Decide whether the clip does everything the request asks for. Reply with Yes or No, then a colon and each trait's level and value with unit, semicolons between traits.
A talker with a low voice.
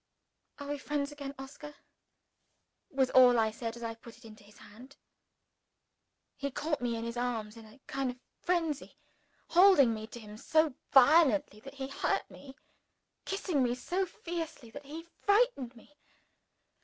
No: very high, 270 Hz